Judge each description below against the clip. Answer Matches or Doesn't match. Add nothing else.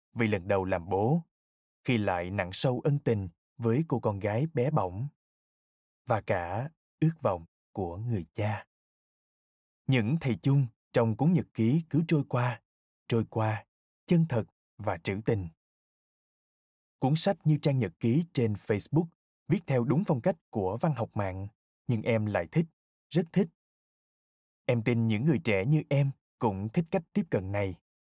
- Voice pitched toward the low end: Matches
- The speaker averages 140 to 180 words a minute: Matches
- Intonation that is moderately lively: Doesn't match